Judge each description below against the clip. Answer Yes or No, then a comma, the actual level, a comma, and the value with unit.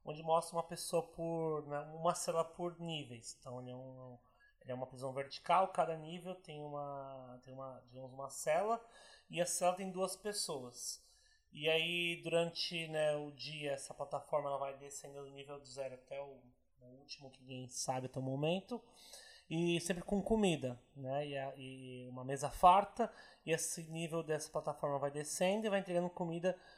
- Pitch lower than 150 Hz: No, medium, 155 Hz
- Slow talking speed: No, average, 180 wpm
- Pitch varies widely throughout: No, average, 4.3 semitones